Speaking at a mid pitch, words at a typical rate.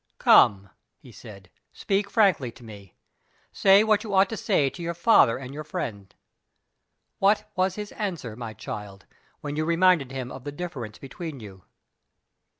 Yes: medium, 145 Hz; average, 160 wpm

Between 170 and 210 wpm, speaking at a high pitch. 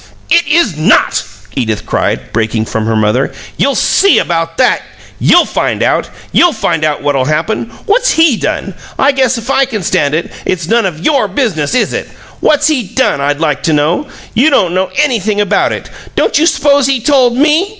Yes: average, 190 wpm; high, 215 Hz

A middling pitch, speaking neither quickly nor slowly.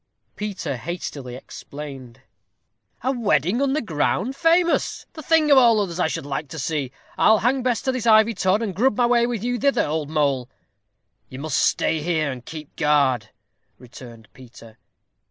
Yes: medium, 170 Hz; average, 170 wpm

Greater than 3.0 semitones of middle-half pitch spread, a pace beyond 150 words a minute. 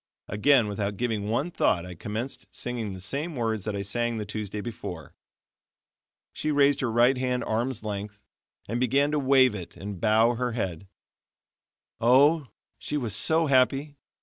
Yes: average, 4.5 semitones; average, 160 wpm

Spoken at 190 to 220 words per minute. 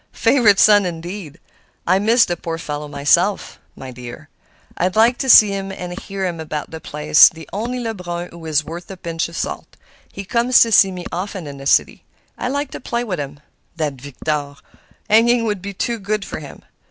Yes: average, 200 wpm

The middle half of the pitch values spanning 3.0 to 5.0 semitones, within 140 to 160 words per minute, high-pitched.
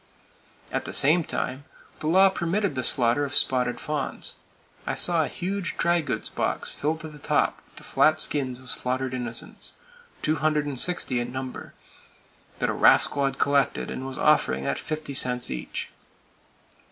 No: average, 3.5 semitones; average, 155 wpm; medium, 140 Hz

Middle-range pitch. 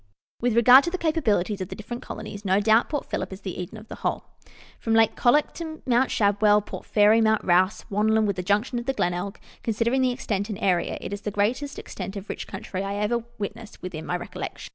No: high, 215 Hz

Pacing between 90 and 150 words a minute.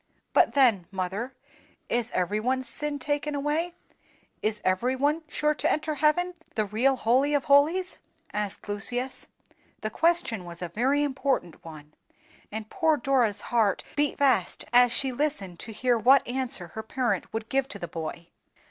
No: average, 160 wpm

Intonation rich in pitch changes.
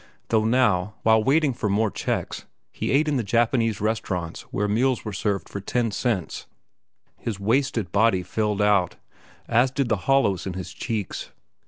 No: average, 3.5 semitones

